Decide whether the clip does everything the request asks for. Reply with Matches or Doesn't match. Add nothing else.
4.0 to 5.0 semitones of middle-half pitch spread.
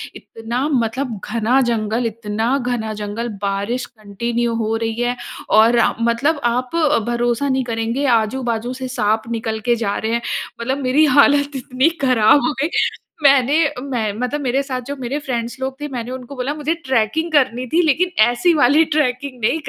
Doesn't match